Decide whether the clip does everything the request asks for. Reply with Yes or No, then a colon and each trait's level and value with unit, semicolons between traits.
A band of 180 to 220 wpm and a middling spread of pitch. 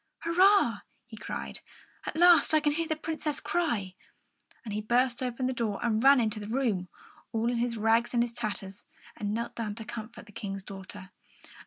Yes: average, 190 wpm; average, 4.1 semitones